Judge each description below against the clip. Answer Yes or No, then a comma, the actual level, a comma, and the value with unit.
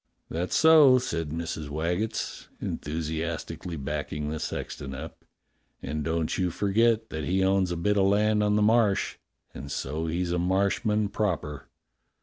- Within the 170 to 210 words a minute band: No, average, 150 wpm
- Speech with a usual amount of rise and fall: Yes, average, 4.8 semitones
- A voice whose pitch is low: Yes, very low, 90 Hz